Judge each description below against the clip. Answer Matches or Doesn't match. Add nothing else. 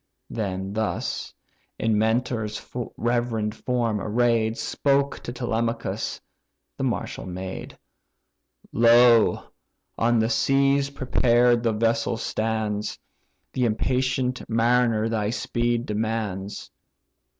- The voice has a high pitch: Doesn't match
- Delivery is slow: Matches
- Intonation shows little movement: Matches